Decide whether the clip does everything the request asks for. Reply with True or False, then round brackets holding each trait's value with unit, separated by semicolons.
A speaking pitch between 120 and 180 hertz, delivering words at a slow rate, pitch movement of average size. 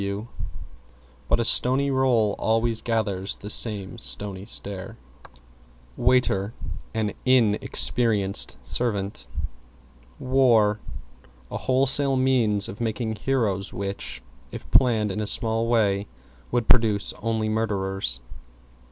False (110 Hz; 105 wpm; 3.2 semitones)